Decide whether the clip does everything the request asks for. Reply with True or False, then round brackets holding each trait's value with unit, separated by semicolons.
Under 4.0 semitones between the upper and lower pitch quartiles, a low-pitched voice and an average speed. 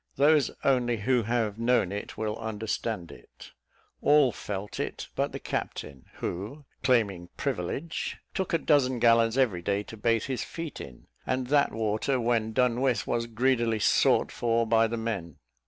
True (3.3 semitones; 115 Hz; 160 wpm)